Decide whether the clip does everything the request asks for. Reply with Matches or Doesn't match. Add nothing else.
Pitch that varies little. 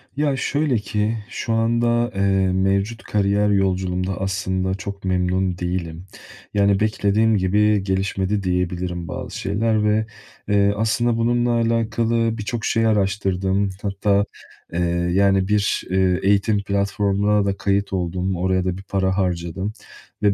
Matches